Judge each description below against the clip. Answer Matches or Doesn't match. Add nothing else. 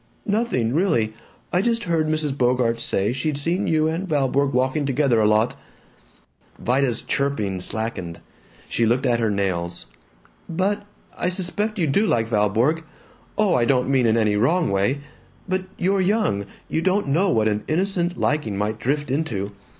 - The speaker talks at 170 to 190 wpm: Doesn't match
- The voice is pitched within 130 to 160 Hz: Matches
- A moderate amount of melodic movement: Doesn't match